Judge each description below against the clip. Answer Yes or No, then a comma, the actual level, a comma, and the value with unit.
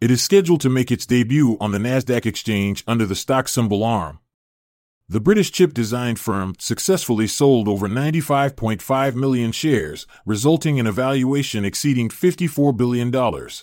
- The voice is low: Yes, low, 125 Hz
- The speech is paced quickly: No, average, 150 wpm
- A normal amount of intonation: Yes, average, 4.2 semitones